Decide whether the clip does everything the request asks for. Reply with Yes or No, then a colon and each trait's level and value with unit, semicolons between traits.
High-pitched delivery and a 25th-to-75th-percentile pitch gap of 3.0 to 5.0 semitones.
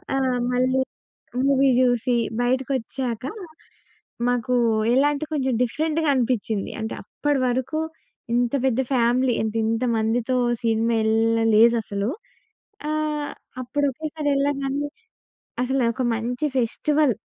Yes: very high, 250 Hz; average, 3.3 semitones